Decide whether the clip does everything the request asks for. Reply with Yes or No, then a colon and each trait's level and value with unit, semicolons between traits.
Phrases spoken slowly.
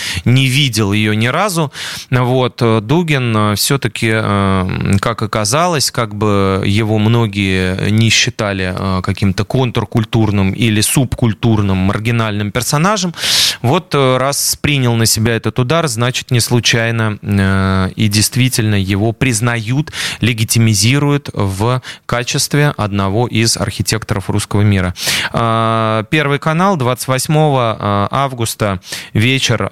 Yes: slow, 100 wpm